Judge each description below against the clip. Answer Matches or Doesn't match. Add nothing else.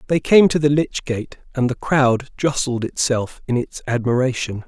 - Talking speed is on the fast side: Doesn't match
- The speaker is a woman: Doesn't match